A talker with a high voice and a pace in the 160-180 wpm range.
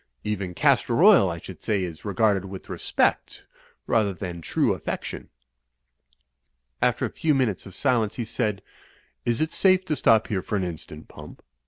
No: low, 105 Hz; average, 170 wpm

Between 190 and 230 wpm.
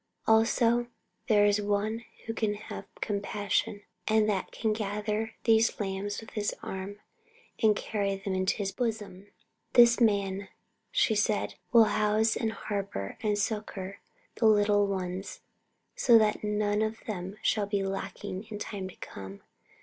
No: average, 150 wpm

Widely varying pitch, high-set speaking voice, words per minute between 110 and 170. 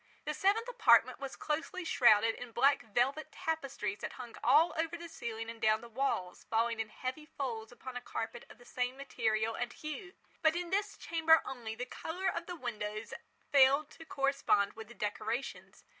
No: wide, 5.9 semitones; very high, 255 Hz; average, 185 wpm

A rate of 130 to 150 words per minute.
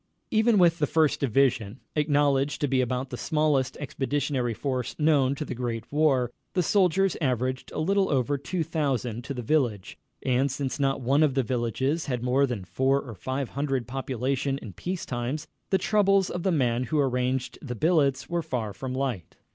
No: average, 185 wpm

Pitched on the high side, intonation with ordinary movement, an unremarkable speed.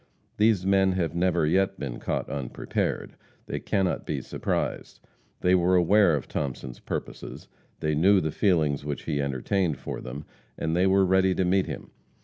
No: very low, 90 Hz; average, 4.5 semitones; average, 165 wpm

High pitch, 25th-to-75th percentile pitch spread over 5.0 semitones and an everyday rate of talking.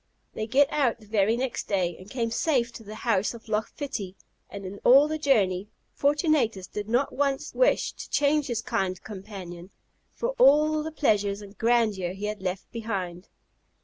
Yes: high, 220 Hz; wide, 5.6 semitones; average, 180 wpm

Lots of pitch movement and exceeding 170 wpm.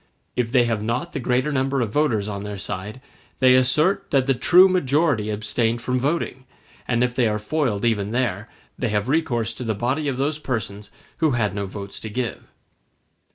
No: average, 4.2 semitones; average, 195 wpm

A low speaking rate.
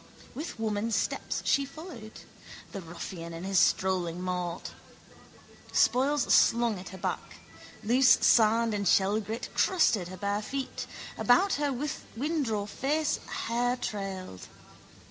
Yes: slow, 120 wpm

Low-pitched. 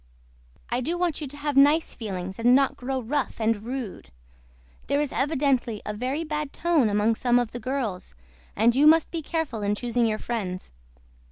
No: very high, 250 Hz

